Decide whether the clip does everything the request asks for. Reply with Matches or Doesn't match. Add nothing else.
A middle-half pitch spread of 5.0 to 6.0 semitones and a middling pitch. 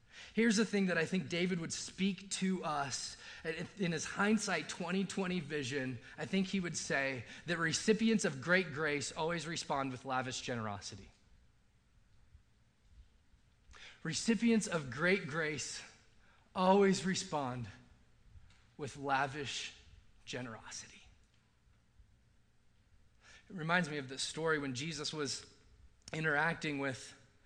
Matches